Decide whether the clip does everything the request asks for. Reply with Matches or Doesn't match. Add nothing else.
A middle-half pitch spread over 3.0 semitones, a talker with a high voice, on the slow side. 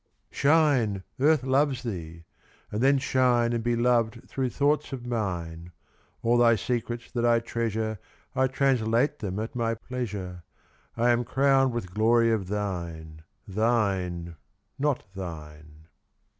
Doesn't match